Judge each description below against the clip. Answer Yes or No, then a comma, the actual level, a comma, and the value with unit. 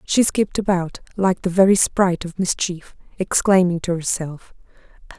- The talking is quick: No, average, 140 wpm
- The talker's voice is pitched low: No, medium, 180 Hz